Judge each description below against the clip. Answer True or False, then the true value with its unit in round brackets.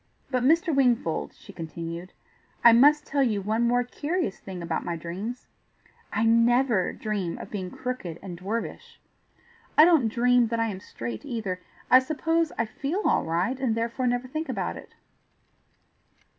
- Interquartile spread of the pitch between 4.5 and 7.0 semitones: True (5.5 semitones)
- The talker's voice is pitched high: True (230 Hz)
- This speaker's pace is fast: False (160 wpm)